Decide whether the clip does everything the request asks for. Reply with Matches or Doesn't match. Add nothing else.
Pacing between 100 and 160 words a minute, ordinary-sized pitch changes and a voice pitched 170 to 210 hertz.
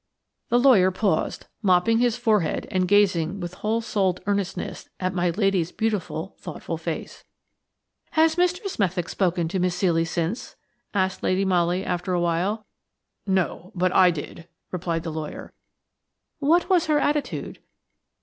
Matches